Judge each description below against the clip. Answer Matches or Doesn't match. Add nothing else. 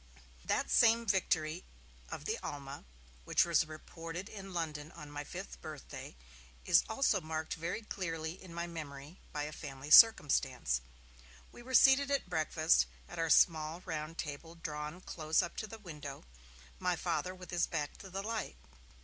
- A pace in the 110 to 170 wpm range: Matches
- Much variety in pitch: Doesn't match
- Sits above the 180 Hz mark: Doesn't match